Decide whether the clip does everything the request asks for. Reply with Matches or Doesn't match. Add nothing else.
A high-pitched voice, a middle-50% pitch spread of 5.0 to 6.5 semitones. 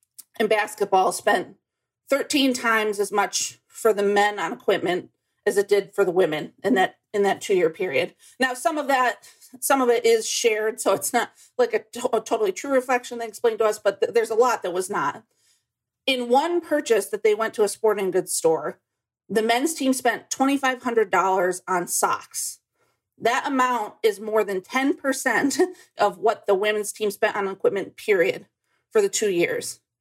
Matches